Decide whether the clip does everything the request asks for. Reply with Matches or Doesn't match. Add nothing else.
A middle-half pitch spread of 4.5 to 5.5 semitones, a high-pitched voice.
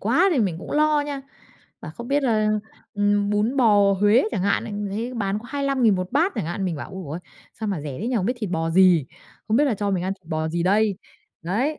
Matches